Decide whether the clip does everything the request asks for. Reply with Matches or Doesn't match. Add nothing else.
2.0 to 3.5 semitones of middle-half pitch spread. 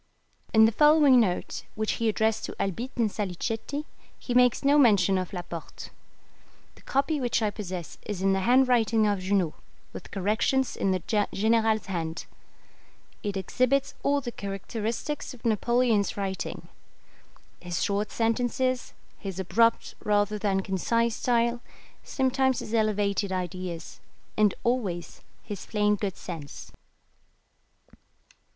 Doesn't match